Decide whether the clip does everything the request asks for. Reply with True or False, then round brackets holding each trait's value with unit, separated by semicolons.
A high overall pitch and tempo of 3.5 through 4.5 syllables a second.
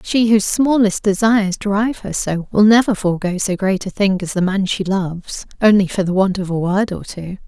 False (200 Hz; 5.4 syllables/s)